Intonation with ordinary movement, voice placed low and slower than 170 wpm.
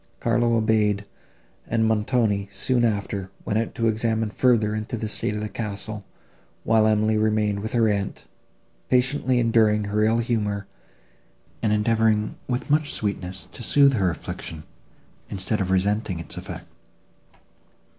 No: narrow, 1.9 semitones; low, 110 Hz; average, 140 wpm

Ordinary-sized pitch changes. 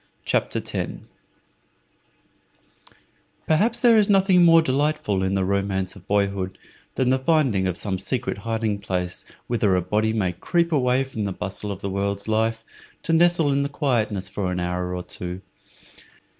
No: wide, 6.8 semitones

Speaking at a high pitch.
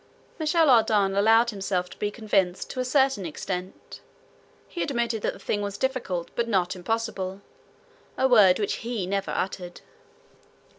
Yes: high, 205 Hz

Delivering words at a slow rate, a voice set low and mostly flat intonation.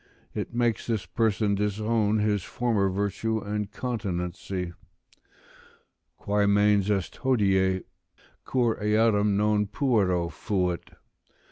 Yes: slow, 100 wpm; low, 105 Hz; narrow, 2.3 semitones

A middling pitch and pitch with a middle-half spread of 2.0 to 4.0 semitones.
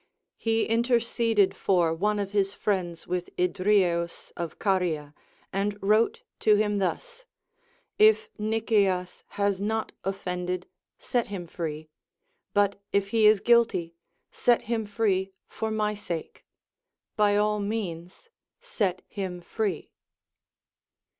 No: high, 200 Hz; average, 3.2 semitones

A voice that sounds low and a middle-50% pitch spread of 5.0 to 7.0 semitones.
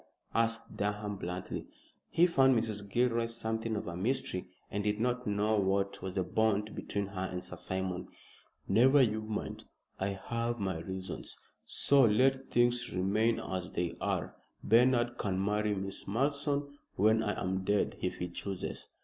No: low, 105 Hz; average, 3.6 semitones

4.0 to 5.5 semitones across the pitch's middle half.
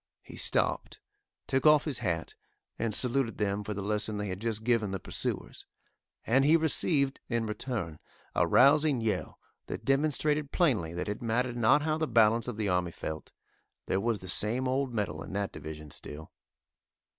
Yes: average, 5.1 semitones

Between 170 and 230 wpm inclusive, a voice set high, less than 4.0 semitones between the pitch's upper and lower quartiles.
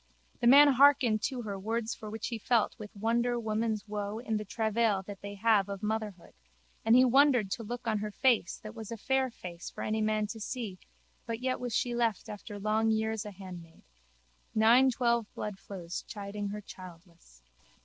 Yes: average, 185 wpm; high, 220 Hz; narrow, 2.6 semitones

